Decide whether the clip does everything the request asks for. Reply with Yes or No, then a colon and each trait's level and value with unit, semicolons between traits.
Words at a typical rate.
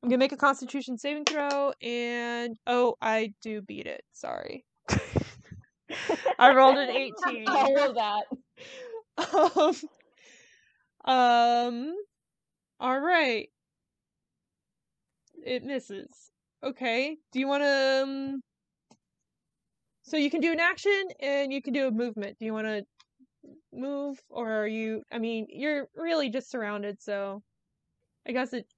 No: slow, 125 wpm